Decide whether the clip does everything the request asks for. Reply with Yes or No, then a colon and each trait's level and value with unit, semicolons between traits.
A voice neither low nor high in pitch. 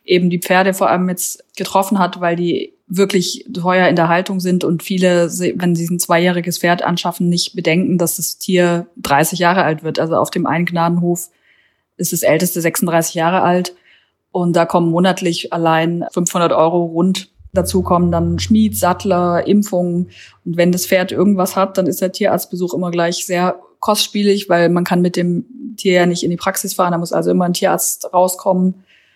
Yes: medium, 180 Hz